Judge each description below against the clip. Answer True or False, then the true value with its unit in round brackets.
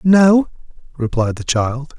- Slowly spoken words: True (120 wpm)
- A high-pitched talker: False (145 Hz)